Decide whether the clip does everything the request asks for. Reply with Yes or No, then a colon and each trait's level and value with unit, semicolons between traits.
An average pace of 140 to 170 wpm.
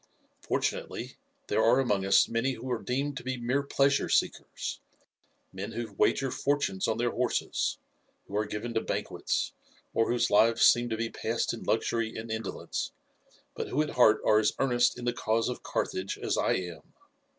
No: average, 180 wpm